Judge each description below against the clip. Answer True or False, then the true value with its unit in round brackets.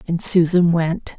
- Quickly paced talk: False (150 wpm)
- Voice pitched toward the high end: False (170 Hz)